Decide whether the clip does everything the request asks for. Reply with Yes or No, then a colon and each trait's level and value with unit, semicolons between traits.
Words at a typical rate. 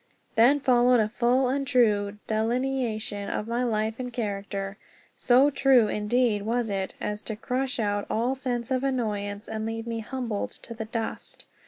Yes: average, 170 wpm